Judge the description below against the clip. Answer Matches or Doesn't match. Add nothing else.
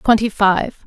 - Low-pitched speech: Doesn't match